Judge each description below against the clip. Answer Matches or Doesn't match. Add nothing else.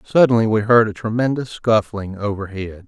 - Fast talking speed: Doesn't match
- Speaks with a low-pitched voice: Matches